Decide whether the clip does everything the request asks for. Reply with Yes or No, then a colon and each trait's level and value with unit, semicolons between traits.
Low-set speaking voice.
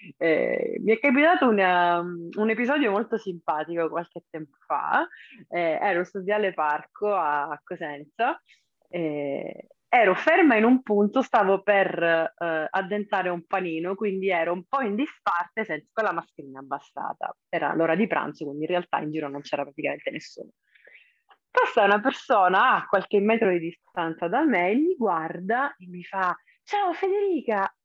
No: high, 190 Hz